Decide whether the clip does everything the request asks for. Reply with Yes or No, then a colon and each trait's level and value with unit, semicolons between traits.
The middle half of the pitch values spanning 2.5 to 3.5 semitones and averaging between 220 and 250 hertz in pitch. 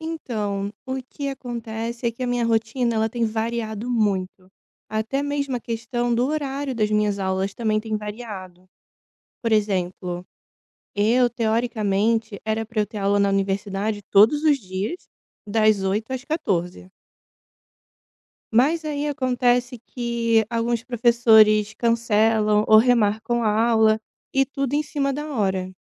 Yes: average, 2.8 semitones; high, 225 Hz